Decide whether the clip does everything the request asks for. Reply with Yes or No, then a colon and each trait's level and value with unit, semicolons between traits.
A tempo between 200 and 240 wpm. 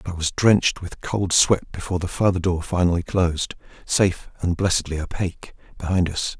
No: average, 180 wpm